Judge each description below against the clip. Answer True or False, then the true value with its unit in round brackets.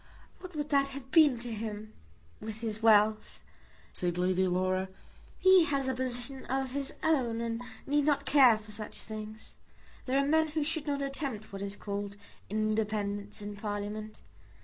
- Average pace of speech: True (165 wpm)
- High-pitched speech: True (225 Hz)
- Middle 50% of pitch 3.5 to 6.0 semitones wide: True (4.9 semitones)